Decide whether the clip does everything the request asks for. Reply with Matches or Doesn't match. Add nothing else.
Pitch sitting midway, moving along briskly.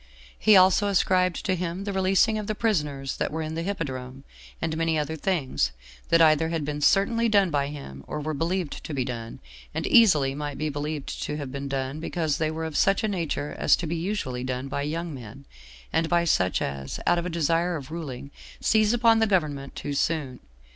Matches